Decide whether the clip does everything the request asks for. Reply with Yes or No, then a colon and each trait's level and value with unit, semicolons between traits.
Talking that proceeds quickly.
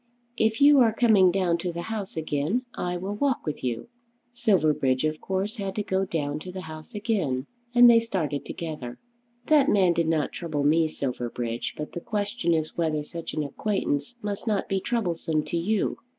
No: average, 185 wpm